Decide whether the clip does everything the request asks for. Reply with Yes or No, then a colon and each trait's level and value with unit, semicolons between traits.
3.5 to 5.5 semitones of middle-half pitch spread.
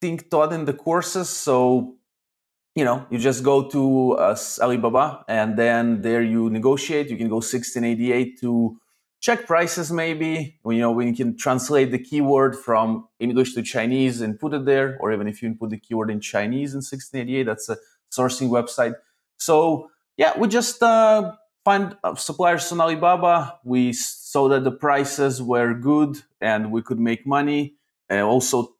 Yes: average, 4.7 semitones